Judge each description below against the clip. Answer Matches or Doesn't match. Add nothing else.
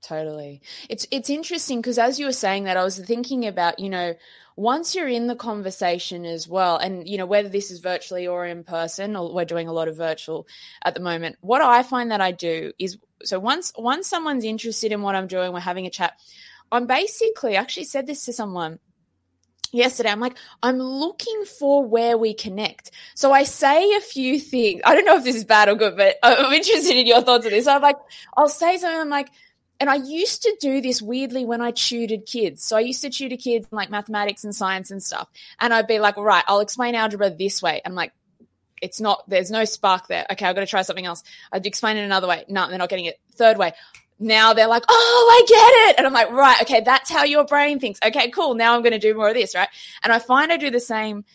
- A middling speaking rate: Doesn't match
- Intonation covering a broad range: Matches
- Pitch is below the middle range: Doesn't match